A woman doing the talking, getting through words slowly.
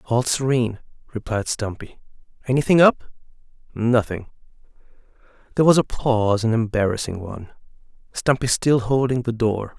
No: male; slow, 105 wpm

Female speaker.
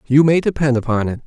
No: male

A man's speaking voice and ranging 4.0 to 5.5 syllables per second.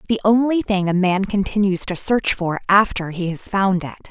No: female; 5.0 syllables/s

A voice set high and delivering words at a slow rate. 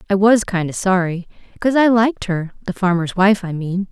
No: high, 195 Hz; average, 200 wpm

